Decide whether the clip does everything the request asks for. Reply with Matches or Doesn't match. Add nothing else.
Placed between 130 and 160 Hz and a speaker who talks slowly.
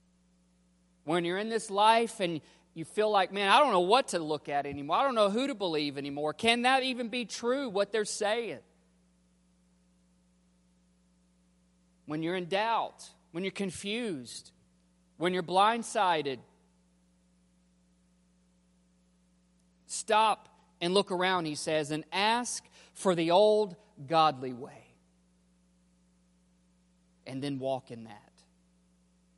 Matches